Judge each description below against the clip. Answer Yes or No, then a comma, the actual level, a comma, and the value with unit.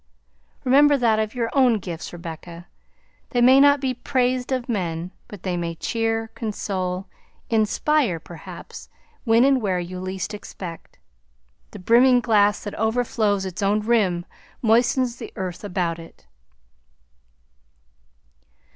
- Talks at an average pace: No, slow, 130 wpm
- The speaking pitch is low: No, high, 215 Hz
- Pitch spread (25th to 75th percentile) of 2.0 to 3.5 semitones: No, average, 5.2 semitones